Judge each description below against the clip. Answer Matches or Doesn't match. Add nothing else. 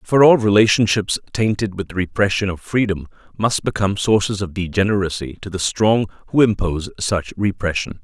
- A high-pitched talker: Doesn't match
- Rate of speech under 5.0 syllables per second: Doesn't match